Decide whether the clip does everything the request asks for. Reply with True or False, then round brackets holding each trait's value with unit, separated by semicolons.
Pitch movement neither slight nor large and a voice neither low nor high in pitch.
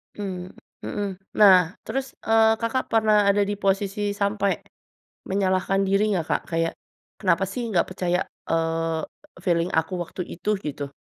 False (3.0 semitones; 195 Hz)